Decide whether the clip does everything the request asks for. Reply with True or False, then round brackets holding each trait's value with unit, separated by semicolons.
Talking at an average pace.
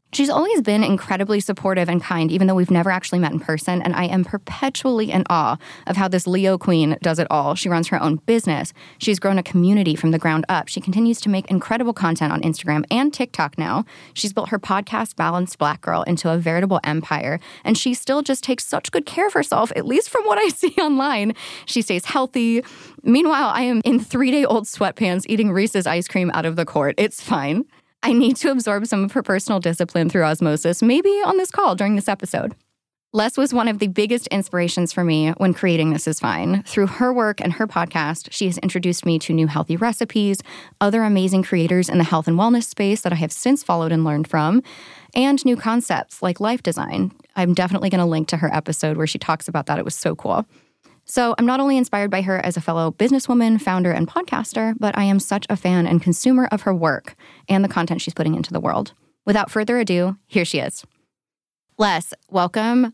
False (220 wpm)